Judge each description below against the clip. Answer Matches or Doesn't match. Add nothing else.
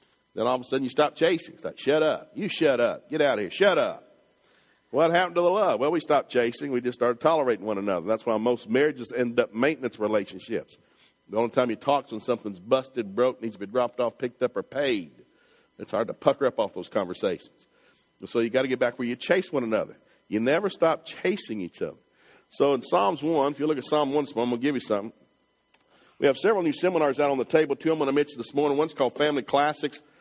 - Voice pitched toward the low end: Matches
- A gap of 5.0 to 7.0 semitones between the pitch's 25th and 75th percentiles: Doesn't match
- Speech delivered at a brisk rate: Matches